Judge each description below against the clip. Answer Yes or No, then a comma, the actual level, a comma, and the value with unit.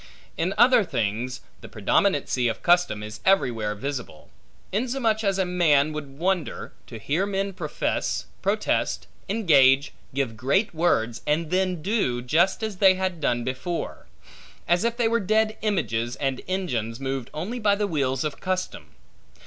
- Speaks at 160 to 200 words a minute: No, average, 150 wpm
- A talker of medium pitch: Yes, medium, 165 Hz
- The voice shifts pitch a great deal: Yes, wide, 7.2 semitones